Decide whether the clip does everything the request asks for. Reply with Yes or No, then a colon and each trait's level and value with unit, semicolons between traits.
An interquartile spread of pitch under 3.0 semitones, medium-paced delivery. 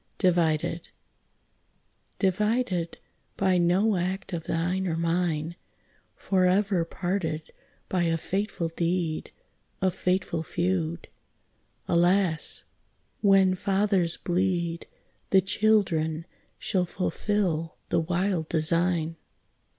No: narrow, 2.4 semitones; slow, 90 wpm